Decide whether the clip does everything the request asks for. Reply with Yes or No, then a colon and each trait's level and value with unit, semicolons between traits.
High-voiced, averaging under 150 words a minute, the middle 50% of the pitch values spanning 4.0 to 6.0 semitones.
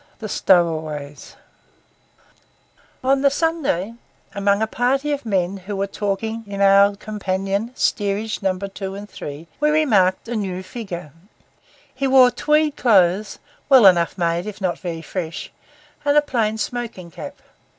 Yes: high, 200 Hz; average, 140 wpm; average, 4.6 semitones